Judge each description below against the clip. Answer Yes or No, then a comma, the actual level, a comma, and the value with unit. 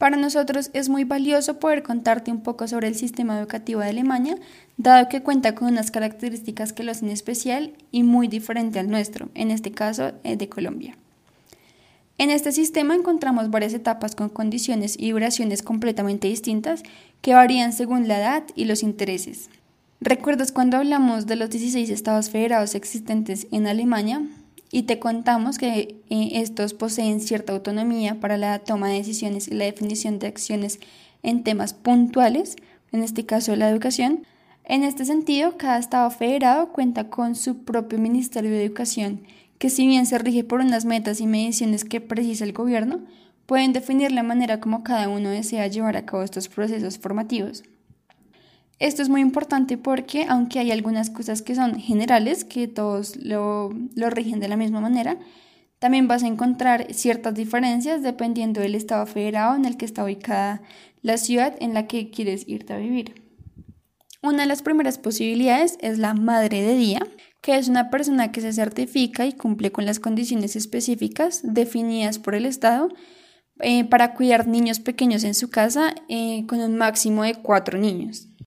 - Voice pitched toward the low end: No, high, 230 Hz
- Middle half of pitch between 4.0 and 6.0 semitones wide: No, average, 2.8 semitones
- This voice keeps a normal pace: Yes, average, 170 wpm